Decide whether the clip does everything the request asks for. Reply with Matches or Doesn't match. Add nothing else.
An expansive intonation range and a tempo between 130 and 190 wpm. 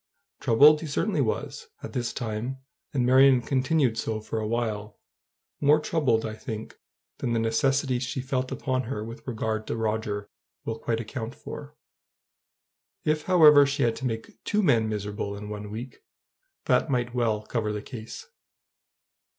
Doesn't match